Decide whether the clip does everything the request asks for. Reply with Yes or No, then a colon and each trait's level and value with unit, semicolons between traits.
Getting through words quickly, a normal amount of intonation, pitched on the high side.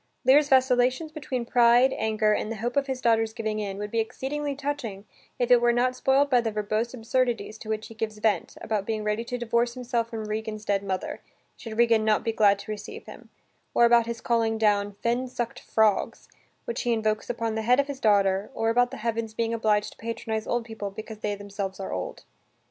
No: fast, 215 wpm; narrow, 2.3 semitones; high, 225 Hz